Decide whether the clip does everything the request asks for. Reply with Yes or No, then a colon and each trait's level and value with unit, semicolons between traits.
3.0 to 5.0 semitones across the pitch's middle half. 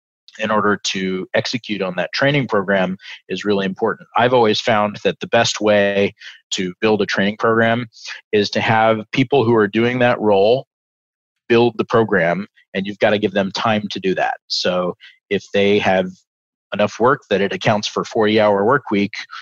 No: narrow, 2.4 semitones